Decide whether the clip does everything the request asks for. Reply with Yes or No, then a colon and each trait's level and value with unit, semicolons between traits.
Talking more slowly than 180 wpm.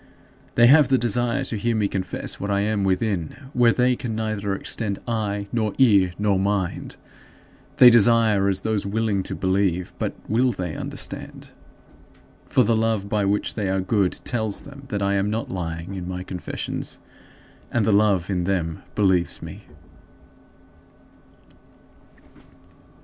Yes: average, 150 wpm